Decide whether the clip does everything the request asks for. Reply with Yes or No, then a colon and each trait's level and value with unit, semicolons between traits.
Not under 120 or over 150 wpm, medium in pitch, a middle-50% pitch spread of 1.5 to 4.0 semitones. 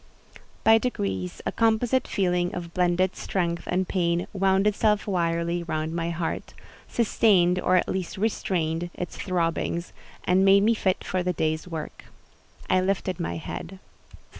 Yes: average, 145 wpm; medium, 180 Hz; narrow, 2.4 semitones